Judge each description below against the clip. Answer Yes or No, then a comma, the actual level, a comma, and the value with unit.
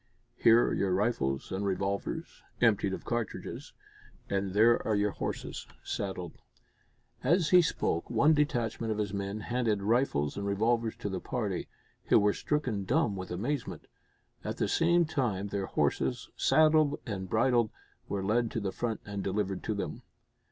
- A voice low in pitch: Yes, low, 105 Hz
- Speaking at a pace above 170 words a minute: No, average, 160 wpm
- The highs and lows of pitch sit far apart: No, average, 3.7 semitones